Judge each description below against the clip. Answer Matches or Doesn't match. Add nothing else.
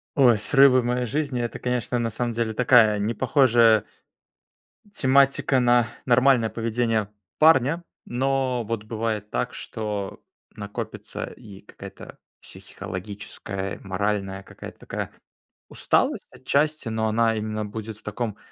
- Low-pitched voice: Matches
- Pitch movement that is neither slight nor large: Matches